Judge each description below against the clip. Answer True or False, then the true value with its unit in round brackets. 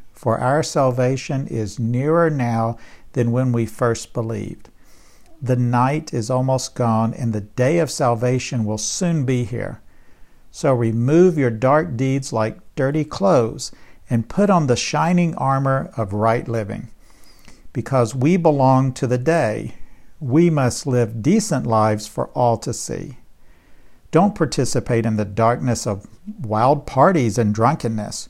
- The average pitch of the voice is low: True (125 Hz)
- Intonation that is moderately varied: True (3.9 semitones)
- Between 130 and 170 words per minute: True (140 wpm)